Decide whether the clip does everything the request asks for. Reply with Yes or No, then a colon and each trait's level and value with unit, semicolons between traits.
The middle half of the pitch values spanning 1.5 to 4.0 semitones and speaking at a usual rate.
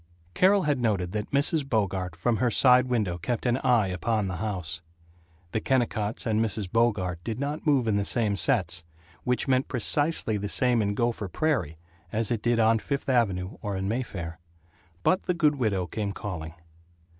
No: average, 4.6 semitones; average, 180 wpm